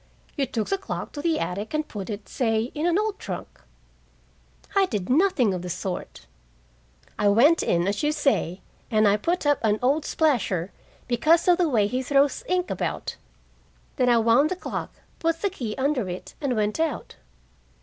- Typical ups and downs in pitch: No, wide, 7.1 semitones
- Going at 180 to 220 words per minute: Yes, average, 190 wpm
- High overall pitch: Yes, very high, 255 Hz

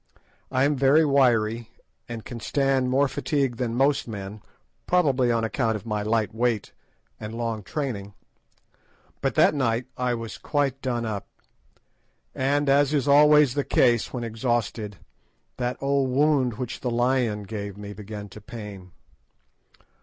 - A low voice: Yes, low, 120 Hz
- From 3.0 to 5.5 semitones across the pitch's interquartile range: Yes, average, 3.8 semitones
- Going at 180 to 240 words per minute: No, average, 155 wpm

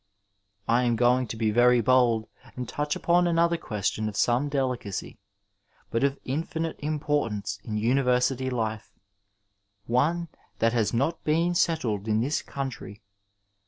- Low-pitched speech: Yes, low, 125 Hz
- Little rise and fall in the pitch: No, average, 4.6 semitones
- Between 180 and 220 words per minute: No, average, 150 wpm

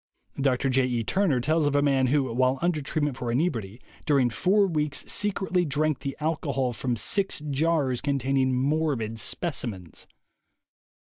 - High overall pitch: No, medium, 140 Hz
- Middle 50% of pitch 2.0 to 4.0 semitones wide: Yes, average, 3.6 semitones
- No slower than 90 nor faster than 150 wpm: Yes, average, 145 wpm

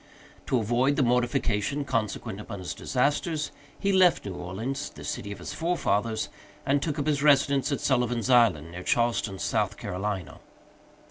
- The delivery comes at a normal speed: Yes, average, 155 wpm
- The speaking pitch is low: Yes, low, 120 Hz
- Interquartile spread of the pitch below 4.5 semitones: No, wide, 5.5 semitones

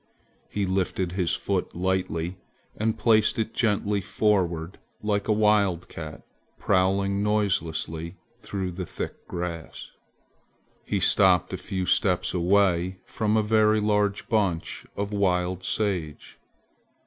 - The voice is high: No, very low, 95 Hz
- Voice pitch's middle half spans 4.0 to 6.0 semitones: No, average, 2.7 semitones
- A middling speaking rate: No, slow, 115 wpm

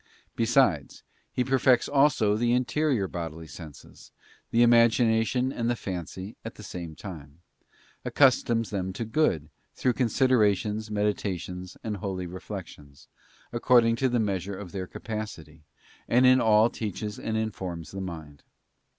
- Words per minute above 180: No, slow, 135 wpm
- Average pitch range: Yes, average, 4.6 semitones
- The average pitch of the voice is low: Yes, low, 105 Hz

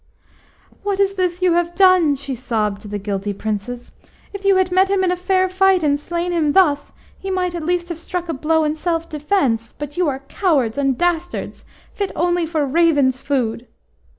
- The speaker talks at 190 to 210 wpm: Yes, average, 195 wpm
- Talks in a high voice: Yes, very high, 330 Hz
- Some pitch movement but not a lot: Yes, average, 5.0 semitones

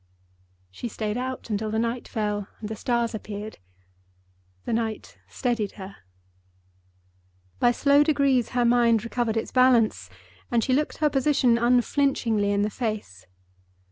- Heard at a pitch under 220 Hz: No, high, 230 Hz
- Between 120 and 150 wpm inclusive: Yes, average, 140 wpm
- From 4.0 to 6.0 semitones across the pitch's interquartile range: No, average, 2.8 semitones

